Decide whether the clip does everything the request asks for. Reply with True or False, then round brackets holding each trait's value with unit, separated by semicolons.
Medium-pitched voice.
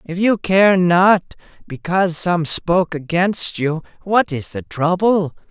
True (175 Hz)